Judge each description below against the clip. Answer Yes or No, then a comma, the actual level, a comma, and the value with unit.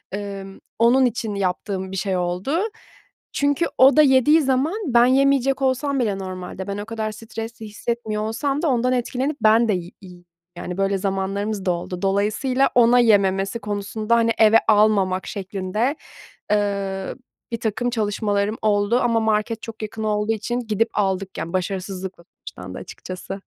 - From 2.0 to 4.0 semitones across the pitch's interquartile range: Yes, average, 3.6 semitones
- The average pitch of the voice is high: Yes, high, 215 Hz